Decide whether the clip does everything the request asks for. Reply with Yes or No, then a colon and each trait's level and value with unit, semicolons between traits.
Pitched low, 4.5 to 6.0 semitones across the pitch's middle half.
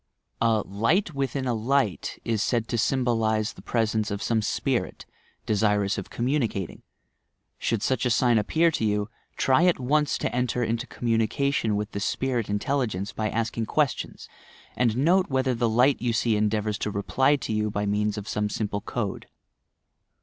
No: low, 115 Hz; average, 3.6 semitones